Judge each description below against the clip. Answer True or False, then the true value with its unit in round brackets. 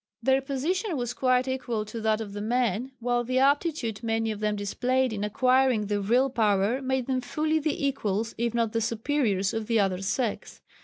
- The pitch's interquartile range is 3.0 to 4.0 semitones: True (3.7 semitones)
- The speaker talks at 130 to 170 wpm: False (195 wpm)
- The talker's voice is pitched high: True (235 Hz)